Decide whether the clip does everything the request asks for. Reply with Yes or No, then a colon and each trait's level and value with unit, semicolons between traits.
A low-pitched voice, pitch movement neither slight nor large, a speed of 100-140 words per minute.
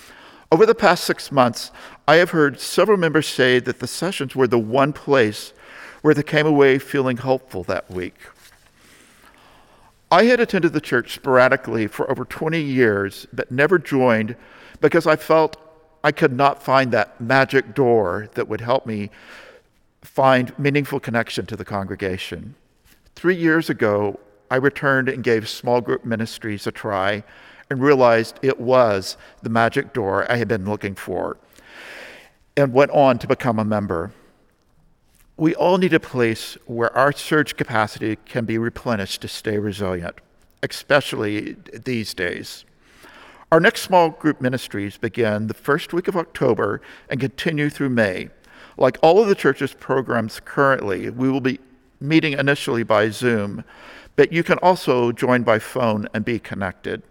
No: low, 130 Hz; average, 4.3 semitones; average, 155 wpm